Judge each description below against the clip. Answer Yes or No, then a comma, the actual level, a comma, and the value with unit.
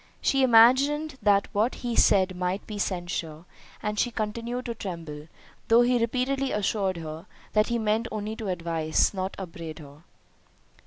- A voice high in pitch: Yes, high, 210 Hz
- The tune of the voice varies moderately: Yes, average, 4.9 semitones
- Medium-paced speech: Yes, average, 155 wpm